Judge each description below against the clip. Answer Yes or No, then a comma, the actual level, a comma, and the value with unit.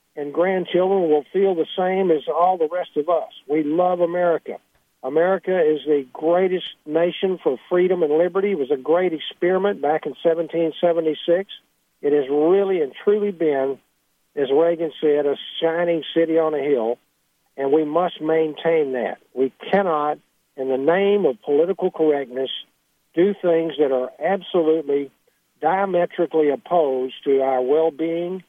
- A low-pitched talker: No, medium, 165 Hz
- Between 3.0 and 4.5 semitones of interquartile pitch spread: Yes, average, 3.5 semitones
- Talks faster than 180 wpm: No, average, 150 wpm